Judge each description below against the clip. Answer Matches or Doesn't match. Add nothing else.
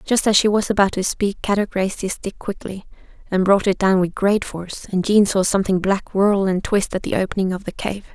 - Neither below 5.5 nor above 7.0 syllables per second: Matches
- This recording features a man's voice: Doesn't match